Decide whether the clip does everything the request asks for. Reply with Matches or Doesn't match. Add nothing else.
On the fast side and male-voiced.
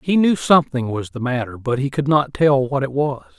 Matches